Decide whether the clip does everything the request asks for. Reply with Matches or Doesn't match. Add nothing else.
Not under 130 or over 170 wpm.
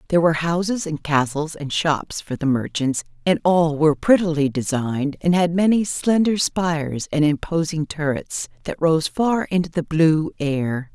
Matches